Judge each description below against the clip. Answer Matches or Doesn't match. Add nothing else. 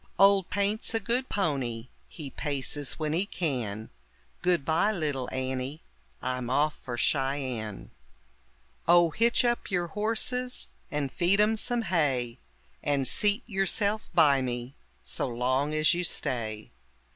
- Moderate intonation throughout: Doesn't match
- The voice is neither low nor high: Matches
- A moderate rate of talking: Doesn't match